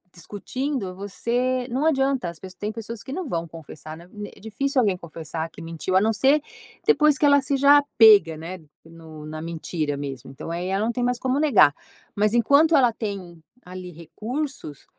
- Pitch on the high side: Yes, high, 205 Hz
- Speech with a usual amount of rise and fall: No, wide, 7.9 semitones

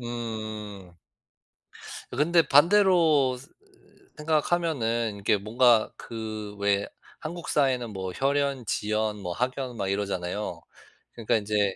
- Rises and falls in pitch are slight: No, average, 5.2 semitones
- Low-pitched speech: Yes, low, 115 Hz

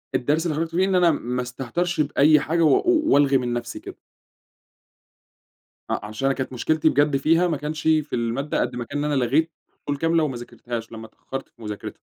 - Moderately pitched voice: Yes, medium, 145 Hz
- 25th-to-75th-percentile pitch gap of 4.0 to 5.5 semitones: Yes, average, 4.5 semitones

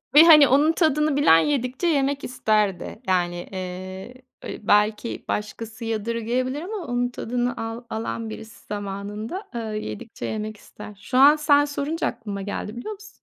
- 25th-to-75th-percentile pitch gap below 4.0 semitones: No, average, 5.2 semitones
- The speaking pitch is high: Yes, high, 235 Hz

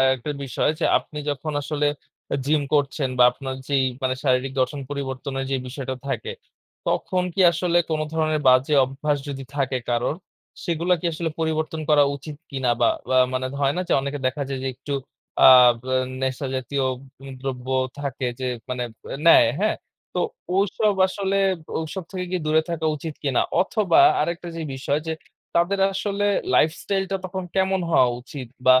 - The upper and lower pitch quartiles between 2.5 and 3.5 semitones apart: No, average, 4.2 semitones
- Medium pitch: Yes, medium, 145 Hz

